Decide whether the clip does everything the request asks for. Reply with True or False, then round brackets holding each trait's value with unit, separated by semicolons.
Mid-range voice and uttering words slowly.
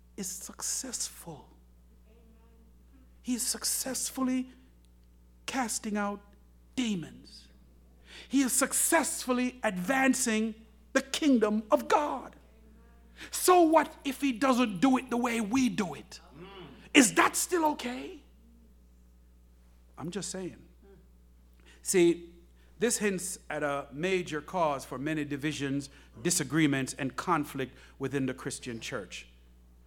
True (155 Hz; 105 wpm)